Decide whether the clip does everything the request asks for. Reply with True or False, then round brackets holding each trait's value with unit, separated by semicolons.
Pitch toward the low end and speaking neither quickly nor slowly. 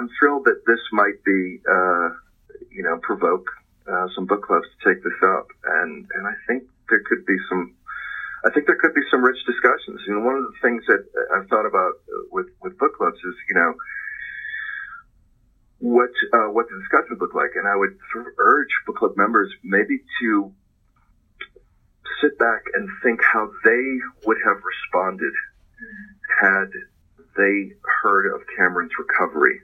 False (330 Hz; 165 wpm)